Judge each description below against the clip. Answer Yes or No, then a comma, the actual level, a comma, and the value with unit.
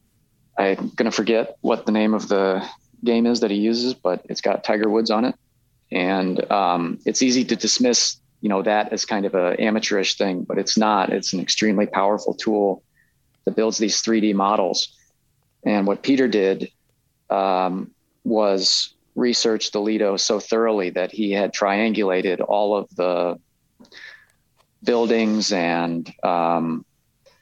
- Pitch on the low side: Yes, low, 105 Hz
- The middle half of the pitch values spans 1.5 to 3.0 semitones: Yes, average, 2.7 semitones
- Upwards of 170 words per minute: No, average, 155 wpm